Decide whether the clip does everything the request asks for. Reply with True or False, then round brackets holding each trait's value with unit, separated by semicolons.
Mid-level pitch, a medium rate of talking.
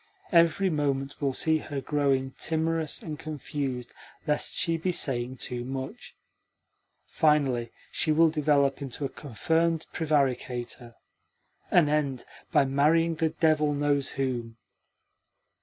False (145 Hz; 120 wpm)